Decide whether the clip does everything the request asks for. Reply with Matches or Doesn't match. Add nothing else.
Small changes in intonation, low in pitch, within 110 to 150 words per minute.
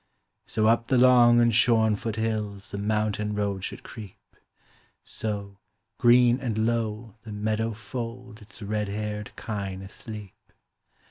Matches